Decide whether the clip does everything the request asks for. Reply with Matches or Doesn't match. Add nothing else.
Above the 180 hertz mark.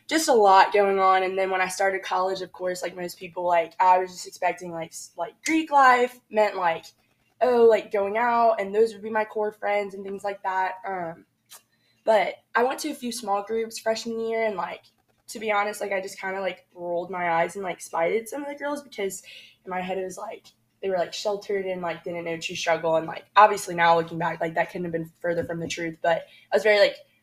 Matches